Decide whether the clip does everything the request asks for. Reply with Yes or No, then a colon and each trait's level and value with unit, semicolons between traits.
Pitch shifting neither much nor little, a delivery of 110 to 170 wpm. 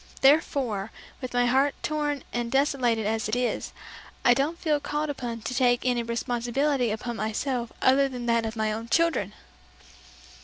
Yes: average, 3.2 semitones; average, 160 wpm